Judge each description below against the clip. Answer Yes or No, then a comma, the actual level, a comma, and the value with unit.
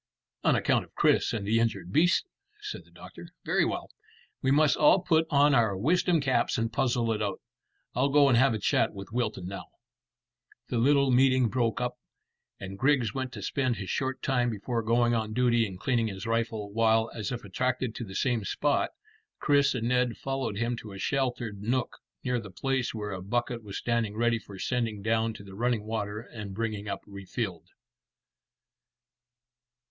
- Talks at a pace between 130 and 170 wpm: No, average, 185 wpm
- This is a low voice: Yes, low, 115 Hz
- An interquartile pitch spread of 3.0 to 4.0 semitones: Yes, average, 3.4 semitones